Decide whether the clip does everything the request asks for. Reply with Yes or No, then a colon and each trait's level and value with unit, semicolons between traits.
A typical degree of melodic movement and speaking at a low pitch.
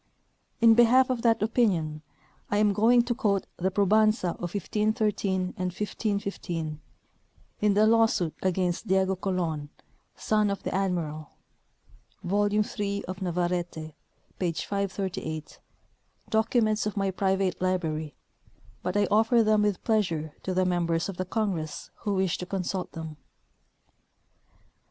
No: average, 3.3 semitones; high, 195 Hz